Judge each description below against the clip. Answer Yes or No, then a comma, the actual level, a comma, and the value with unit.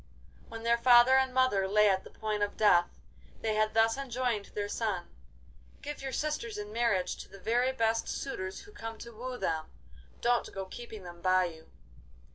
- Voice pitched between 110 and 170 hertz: No, high, 225 Hz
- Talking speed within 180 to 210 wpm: Yes, average, 185 wpm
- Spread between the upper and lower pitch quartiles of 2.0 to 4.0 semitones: Yes, average, 3.7 semitones